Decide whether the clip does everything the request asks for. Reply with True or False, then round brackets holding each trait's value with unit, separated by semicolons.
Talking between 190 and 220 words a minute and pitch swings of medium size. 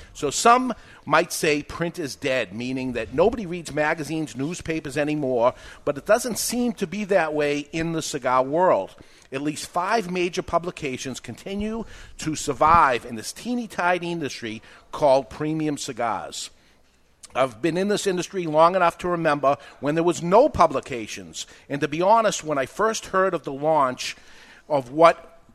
False (160 wpm; 4.0 semitones)